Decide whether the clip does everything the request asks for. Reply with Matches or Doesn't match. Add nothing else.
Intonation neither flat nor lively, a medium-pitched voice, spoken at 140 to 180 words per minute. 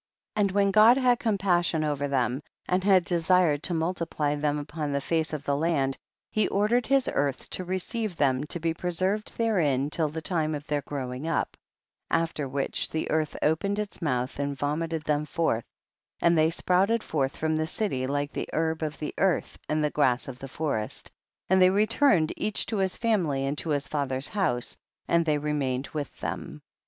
Doesn't match